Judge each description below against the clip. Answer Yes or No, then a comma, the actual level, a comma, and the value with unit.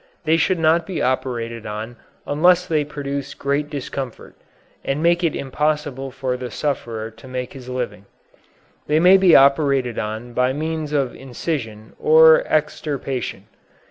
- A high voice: No, medium, 140 Hz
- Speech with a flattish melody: No, average, 3.8 semitones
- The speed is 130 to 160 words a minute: Yes, average, 140 wpm